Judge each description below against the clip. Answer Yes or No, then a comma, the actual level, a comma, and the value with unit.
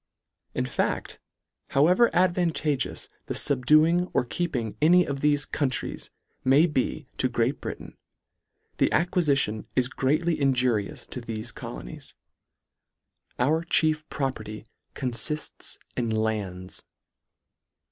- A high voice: No, low, 135 Hz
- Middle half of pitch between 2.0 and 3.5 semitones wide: No, average, 4.9 semitones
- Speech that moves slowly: Yes, slow, 105 wpm